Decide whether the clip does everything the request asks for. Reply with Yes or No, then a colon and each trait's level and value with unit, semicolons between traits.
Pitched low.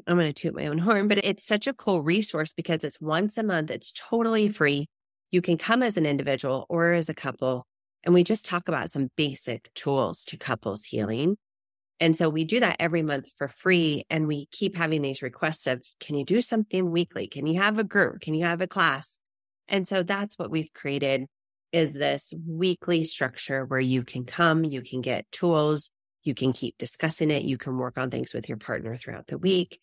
No: medium, 160 Hz